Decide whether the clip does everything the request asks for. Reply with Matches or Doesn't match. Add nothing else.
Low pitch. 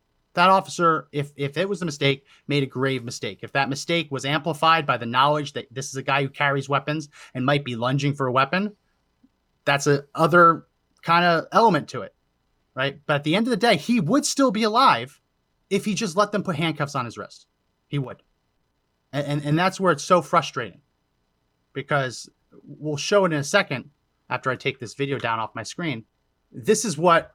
Doesn't match